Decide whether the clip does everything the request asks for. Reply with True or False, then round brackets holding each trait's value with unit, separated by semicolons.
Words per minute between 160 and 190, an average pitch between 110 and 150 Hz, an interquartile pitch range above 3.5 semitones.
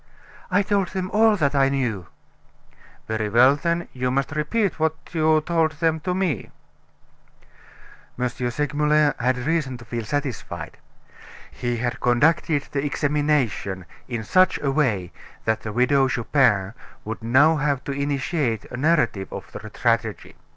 False (145 wpm; 140 Hz; 4.7 semitones)